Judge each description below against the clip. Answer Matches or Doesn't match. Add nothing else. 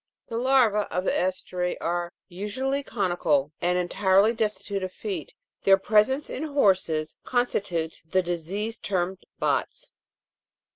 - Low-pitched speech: Doesn't match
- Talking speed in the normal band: Doesn't match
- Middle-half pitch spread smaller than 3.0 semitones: Doesn't match